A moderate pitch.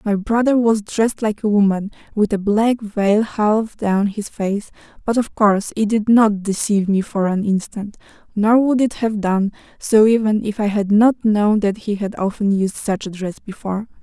No: high, 210 Hz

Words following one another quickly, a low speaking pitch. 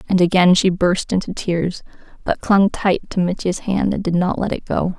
No: fast, 215 wpm; medium, 185 Hz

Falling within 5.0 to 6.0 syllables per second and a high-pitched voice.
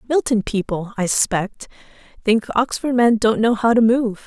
No: 4.6 syllables/s; high, 225 Hz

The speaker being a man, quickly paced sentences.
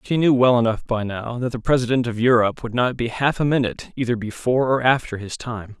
Yes: male; fast, 240 wpm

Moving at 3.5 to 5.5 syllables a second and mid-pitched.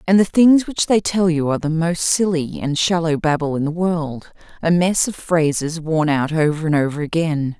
Yes: 4.9 syllables/s; medium, 165 Hz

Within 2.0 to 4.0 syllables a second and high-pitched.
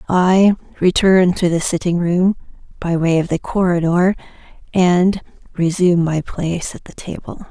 No: 3.8 syllables/s; medium, 175 Hz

